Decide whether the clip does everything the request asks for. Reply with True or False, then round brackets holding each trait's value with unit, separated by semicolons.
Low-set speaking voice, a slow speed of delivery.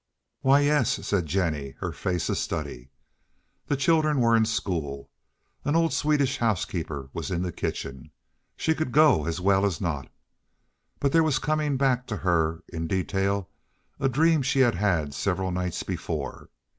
False (100 Hz; 160 wpm)